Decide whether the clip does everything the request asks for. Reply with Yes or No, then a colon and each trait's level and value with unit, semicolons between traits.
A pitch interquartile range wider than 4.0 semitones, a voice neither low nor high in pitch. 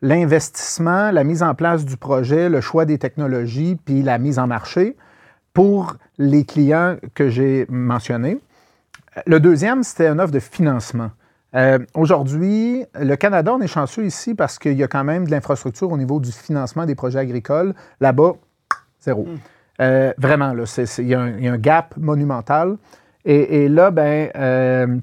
Yes: average, 4.6 semitones; medium, 145 Hz